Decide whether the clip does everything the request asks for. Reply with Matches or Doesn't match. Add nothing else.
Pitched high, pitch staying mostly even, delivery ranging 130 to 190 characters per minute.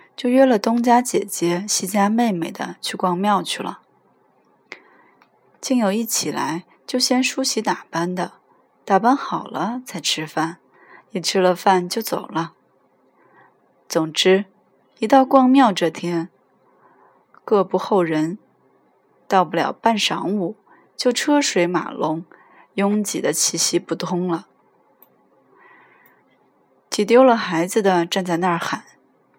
Doesn't match